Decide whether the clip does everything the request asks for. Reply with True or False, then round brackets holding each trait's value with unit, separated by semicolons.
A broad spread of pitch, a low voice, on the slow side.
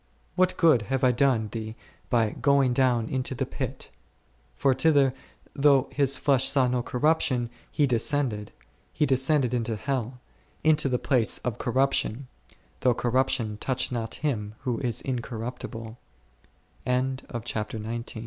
False (2.9 semitones; 130 Hz; 120 wpm)